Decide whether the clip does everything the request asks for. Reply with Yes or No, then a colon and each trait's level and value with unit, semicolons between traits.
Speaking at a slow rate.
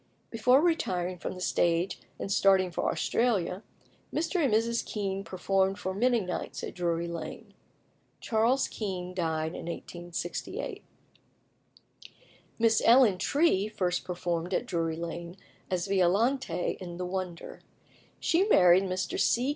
Yes: slow, 130 wpm